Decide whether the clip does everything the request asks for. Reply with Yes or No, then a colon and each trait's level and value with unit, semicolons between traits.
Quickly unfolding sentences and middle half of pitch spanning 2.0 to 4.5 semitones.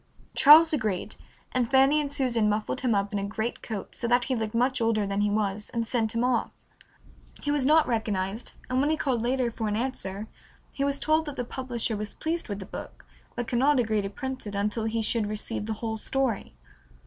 Yes: fast, 220 wpm; average, 3.8 semitones